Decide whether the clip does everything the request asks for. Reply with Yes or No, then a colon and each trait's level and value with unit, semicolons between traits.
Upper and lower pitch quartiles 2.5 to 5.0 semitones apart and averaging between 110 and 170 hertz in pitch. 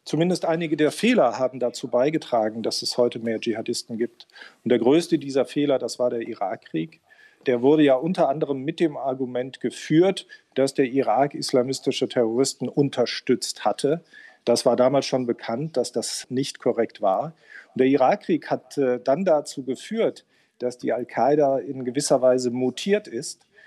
Yes: average, 3.3 semitones; low, 135 Hz